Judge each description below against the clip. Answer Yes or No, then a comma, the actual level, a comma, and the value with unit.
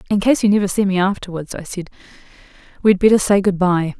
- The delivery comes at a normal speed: No, fast, 210 wpm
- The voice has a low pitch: No, high, 190 Hz